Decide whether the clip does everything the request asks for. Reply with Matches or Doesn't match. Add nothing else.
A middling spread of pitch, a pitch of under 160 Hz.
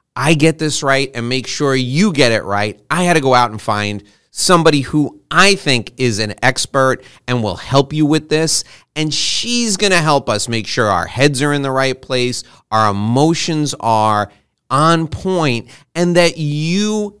Matches